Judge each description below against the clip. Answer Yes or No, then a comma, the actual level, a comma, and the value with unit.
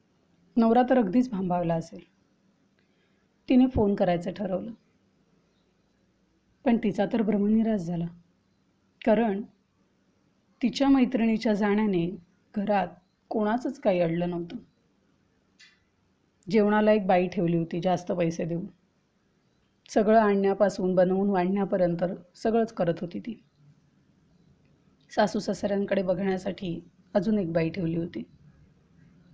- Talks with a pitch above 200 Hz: No, high, 195 Hz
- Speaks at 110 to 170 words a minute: No, average, 95 wpm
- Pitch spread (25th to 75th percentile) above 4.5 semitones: No, average, 3.7 semitones